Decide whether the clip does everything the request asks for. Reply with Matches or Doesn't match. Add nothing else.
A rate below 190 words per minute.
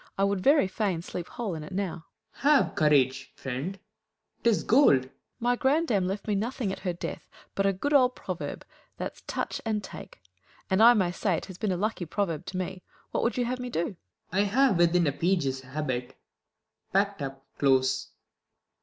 Doesn't match